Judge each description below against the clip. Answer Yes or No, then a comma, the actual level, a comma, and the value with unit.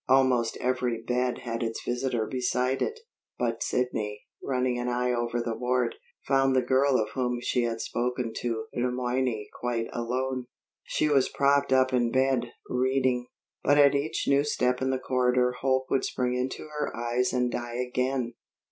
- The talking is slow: No, average, 170 wpm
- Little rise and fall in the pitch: Yes, narrow, 1.4 semitones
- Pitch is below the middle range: Yes, low, 125 Hz